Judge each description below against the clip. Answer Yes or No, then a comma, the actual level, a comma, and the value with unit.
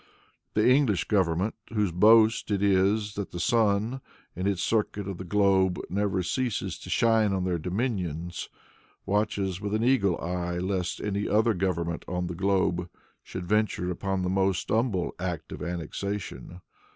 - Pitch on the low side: Yes, very low, 95 Hz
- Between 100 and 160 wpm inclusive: Yes, average, 155 wpm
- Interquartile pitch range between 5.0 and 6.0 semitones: No, average, 2.9 semitones